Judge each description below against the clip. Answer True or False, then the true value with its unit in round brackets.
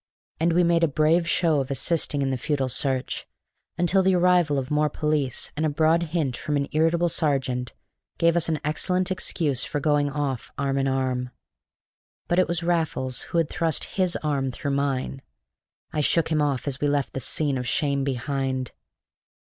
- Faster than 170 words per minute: True (185 wpm)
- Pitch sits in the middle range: True (150 Hz)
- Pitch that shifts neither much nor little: True (3.6 semitones)